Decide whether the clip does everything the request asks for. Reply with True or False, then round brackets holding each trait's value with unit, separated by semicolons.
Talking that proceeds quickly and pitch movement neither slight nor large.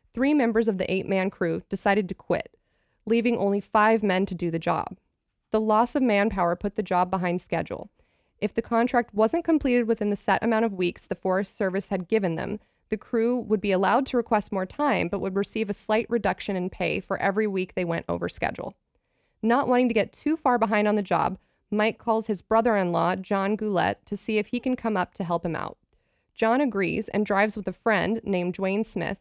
True (215 wpm; 3.1 semitones)